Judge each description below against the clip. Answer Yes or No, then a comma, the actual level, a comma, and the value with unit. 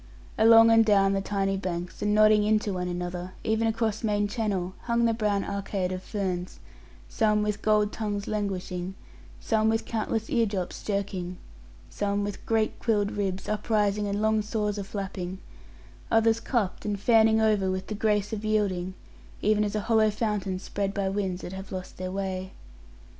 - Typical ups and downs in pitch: No, narrow, 2.1 semitones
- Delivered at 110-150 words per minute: No, average, 170 wpm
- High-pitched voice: Yes, high, 205 Hz